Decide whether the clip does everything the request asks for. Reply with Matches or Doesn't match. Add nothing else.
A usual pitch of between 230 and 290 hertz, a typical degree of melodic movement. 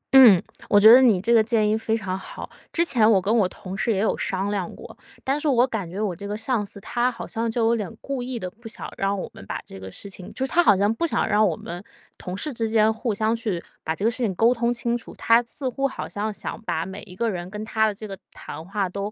Doesn't match